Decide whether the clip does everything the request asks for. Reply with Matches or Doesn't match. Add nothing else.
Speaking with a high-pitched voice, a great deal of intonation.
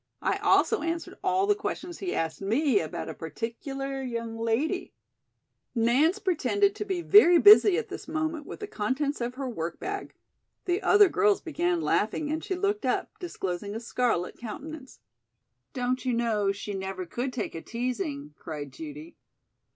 Matches